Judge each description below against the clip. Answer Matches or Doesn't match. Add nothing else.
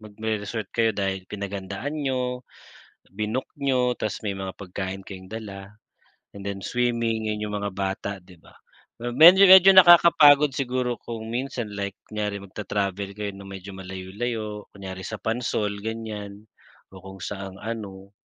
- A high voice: Doesn't match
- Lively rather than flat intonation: Doesn't match